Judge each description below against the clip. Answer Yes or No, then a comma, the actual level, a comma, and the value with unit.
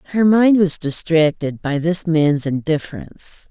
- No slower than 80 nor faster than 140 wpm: Yes, slow, 135 wpm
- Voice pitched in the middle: Yes, medium, 165 Hz